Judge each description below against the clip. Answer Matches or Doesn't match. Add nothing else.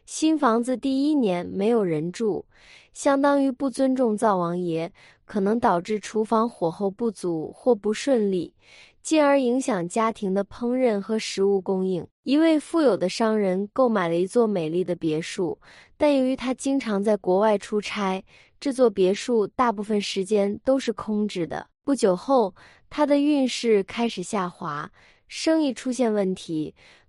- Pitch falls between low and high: Doesn't match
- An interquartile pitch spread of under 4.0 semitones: Doesn't match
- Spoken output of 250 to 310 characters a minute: Doesn't match